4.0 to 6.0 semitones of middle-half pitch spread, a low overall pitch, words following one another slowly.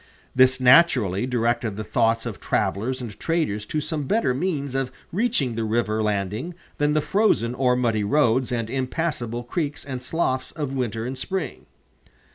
No: average, 4.3 semitones; low, 125 Hz; average, 160 wpm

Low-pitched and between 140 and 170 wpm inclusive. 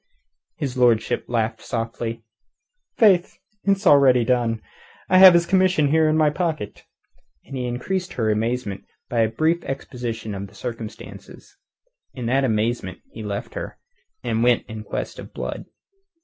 Yes: low, 125 Hz; average, 145 wpm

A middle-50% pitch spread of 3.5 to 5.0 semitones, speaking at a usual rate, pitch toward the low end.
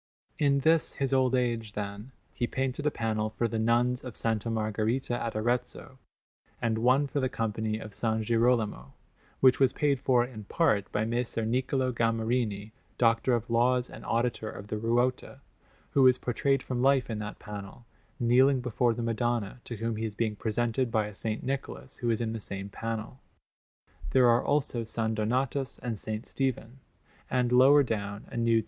No: narrow, 2.5 semitones; average, 180 wpm; low, 120 Hz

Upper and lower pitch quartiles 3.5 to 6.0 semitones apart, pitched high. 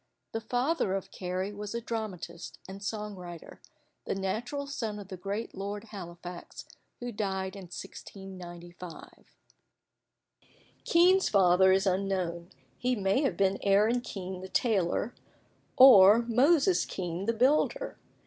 Yes: average, 3.9 semitones; high, 200 Hz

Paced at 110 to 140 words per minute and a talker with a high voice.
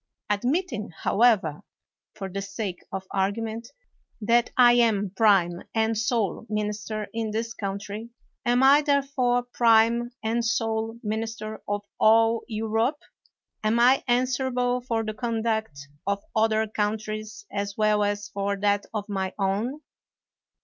Yes: slow, 135 wpm; high, 220 Hz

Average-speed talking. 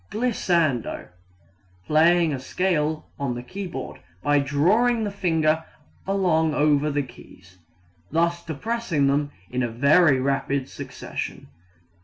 No: slow, 110 wpm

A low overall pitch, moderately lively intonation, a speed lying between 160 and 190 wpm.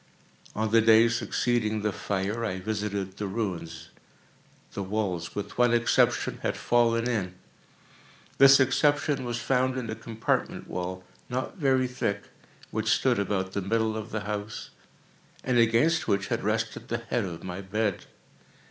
No: low, 110 Hz; average, 3.1 semitones; average, 150 wpm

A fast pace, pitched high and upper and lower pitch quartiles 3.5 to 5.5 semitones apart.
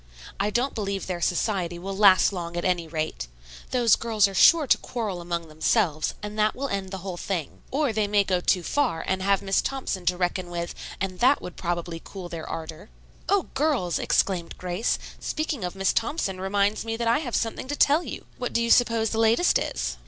Yes: fast, 210 wpm; high, 195 Hz; average, 4.7 semitones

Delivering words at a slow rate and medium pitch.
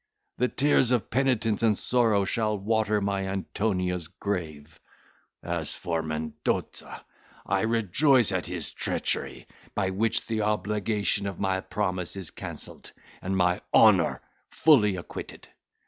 No: slow, 125 wpm; low, 100 Hz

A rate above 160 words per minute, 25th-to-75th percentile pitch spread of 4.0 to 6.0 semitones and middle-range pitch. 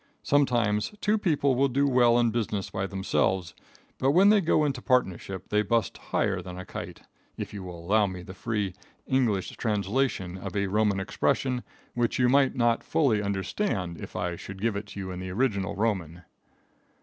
No: average, 180 wpm; average, 5.0 semitones; low, 105 Hz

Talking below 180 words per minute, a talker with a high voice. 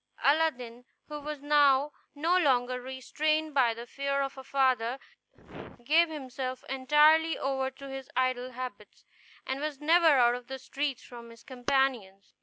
Yes: average, 150 wpm; very high, 265 Hz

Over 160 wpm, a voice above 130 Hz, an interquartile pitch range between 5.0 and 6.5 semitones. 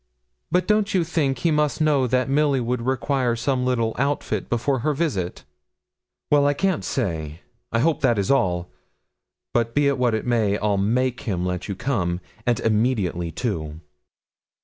No: average, 170 wpm; low, 125 Hz; wide, 5.4 semitones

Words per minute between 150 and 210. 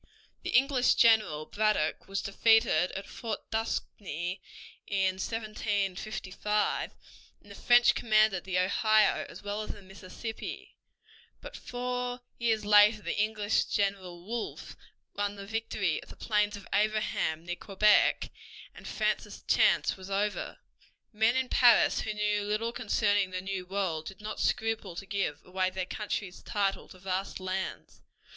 No: average, 140 wpm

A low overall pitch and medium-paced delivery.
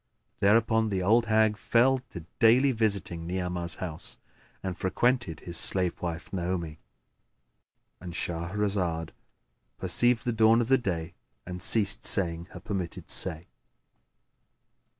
No: very low, 95 Hz; slow, 115 wpm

